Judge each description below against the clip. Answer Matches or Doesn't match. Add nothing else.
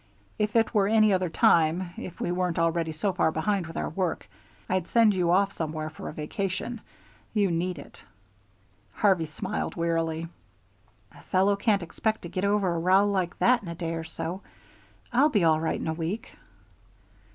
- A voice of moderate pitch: Matches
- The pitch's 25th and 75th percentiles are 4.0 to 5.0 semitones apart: Doesn't match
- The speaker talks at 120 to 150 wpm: Doesn't match